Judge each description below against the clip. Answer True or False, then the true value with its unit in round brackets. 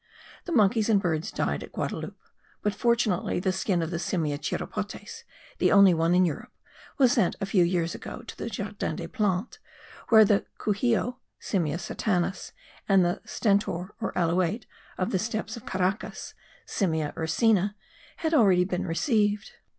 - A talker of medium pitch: False (195 Hz)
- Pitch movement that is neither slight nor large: True (3.7 semitones)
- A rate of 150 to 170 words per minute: True (160 wpm)